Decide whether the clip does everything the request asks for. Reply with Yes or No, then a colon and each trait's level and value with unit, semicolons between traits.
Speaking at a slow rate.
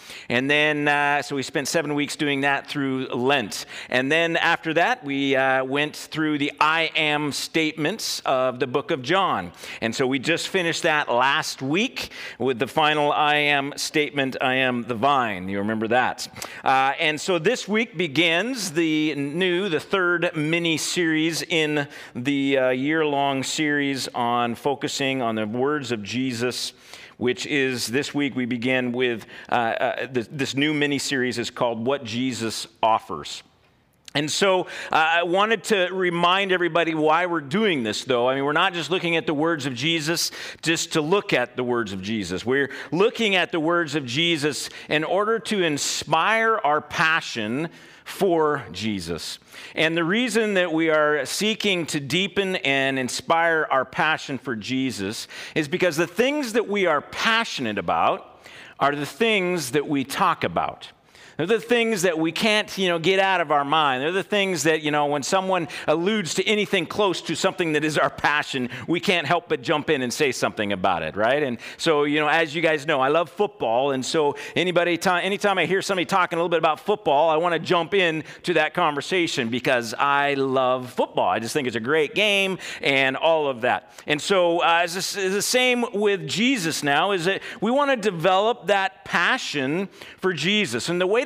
No: average, 185 wpm